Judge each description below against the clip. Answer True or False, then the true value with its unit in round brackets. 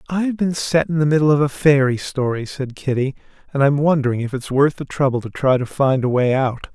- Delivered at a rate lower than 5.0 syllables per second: False (5.7 syllables/s)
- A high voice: False (140 Hz)